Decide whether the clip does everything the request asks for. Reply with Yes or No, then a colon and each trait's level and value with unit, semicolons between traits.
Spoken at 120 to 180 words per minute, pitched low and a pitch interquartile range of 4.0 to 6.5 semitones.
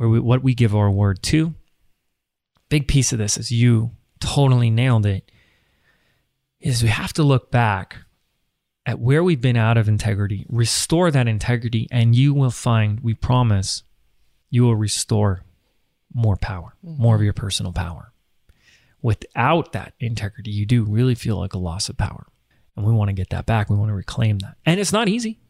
No: average, 175 wpm; low, 115 Hz; average, 3.5 semitones